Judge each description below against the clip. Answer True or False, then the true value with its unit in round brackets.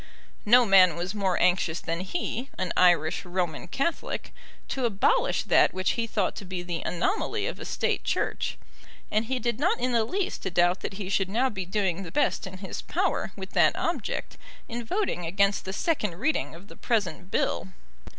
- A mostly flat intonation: False (4.8 semitones)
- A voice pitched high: True (195 Hz)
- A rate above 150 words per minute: True (190 wpm)